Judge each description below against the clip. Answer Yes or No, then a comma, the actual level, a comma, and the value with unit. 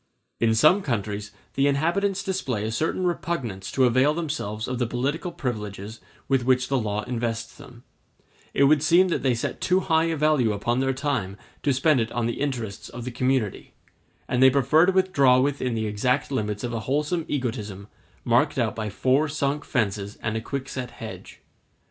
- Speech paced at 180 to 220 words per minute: Yes, average, 185 wpm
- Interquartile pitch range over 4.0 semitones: Yes, average, 4.7 semitones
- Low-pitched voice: Yes, low, 130 Hz